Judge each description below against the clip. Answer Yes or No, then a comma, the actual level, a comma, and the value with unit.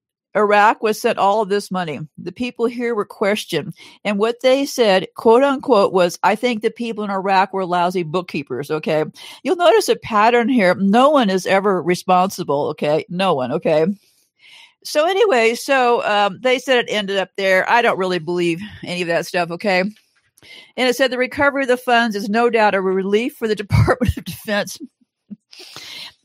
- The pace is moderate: Yes, average, 185 wpm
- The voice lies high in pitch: Yes, high, 210 Hz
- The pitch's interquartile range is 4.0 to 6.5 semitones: Yes, average, 4.8 semitones